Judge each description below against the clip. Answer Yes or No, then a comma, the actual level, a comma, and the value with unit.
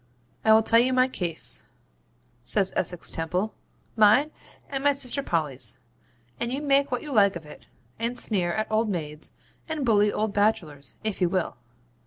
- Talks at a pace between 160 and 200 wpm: Yes, average, 175 wpm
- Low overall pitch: No, high, 215 Hz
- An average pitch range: No, wide, 6.2 semitones